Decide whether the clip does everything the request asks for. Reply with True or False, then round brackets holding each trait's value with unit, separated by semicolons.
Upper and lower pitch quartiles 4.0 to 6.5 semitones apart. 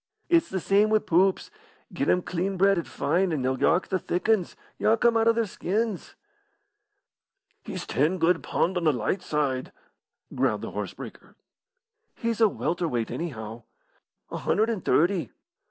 True (4.5 semitones)